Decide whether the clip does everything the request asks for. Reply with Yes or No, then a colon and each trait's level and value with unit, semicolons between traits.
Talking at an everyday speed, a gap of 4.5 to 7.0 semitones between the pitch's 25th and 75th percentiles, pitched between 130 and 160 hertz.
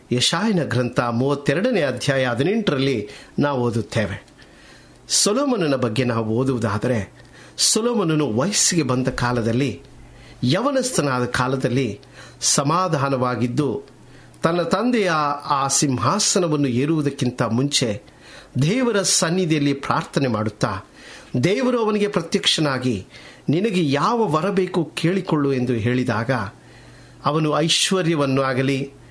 Yes: average, 80 wpm; wide, 5.4 semitones; medium, 140 Hz